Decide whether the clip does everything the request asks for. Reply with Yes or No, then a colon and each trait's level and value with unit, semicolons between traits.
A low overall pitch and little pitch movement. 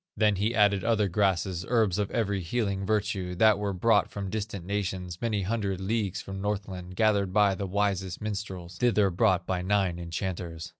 Yes: low, 100 Hz; narrow, 2.3 semitones